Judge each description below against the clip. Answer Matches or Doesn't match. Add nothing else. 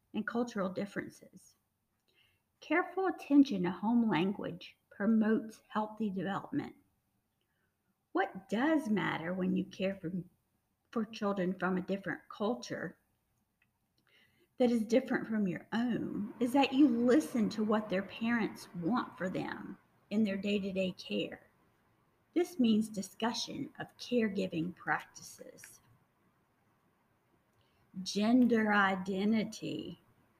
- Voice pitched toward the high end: Matches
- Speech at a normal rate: Doesn't match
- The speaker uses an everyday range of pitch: Matches